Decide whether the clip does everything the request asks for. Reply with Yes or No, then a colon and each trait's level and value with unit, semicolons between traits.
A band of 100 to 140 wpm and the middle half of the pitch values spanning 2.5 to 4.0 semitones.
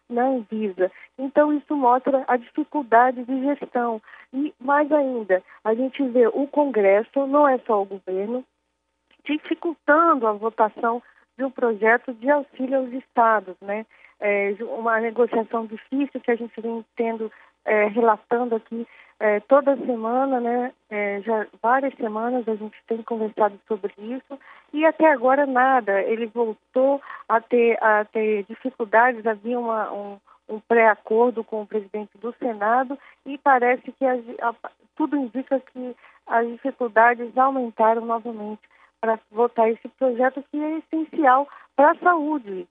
Yes: average, 130 wpm; average, 3.4 semitones